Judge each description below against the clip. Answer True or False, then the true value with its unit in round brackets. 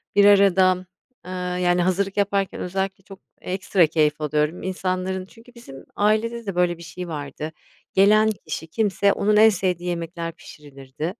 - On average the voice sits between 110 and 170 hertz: False (185 Hz)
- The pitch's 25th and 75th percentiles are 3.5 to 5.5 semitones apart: False (3.0 semitones)